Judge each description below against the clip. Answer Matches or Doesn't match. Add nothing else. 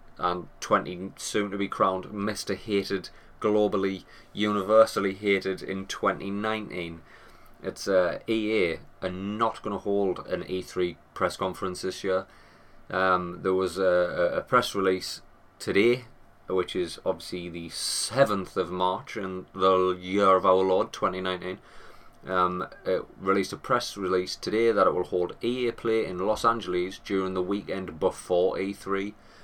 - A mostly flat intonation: Matches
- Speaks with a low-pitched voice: Matches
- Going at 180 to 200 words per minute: Doesn't match